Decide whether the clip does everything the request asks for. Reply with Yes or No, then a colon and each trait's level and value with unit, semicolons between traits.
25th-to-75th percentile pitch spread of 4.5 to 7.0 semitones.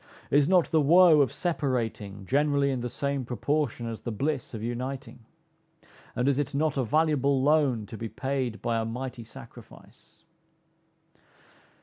No: average, 3.7 semitones